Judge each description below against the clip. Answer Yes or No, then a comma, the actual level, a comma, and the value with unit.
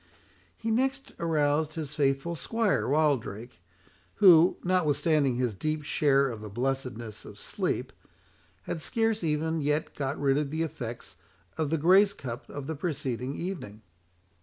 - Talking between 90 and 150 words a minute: Yes, average, 140 wpm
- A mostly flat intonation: No, average, 3.6 semitones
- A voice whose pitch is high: No, medium, 150 Hz